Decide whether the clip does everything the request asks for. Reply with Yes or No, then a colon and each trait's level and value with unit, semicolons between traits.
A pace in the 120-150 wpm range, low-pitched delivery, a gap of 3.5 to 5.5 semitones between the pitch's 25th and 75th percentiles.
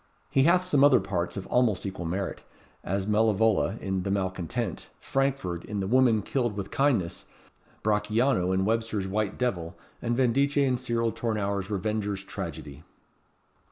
Yes: average, 145 wpm; low, 105 Hz; average, 4.4 semitones